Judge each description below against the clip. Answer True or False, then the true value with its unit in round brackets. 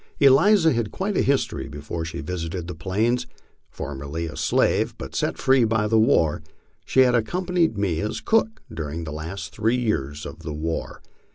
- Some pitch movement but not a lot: False (7.9 semitones)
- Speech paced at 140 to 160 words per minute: False (175 wpm)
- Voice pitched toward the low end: True (105 Hz)